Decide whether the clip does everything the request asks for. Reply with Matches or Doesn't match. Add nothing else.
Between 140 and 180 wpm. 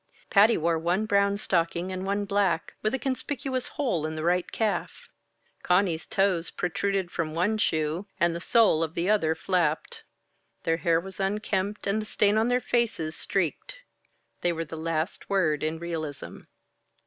Matches